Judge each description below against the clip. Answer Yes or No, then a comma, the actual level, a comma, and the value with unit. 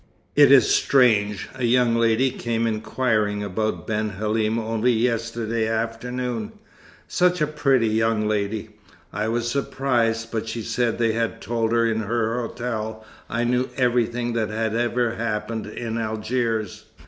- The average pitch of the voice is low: Yes, low, 115 Hz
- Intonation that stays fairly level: Yes, narrow, 1.7 semitones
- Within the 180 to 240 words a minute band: No, average, 145 wpm